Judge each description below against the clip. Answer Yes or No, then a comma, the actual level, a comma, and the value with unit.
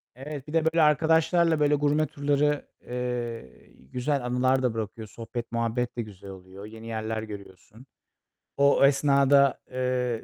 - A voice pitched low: Yes, low, 125 Hz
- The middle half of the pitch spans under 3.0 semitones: No, average, 4.4 semitones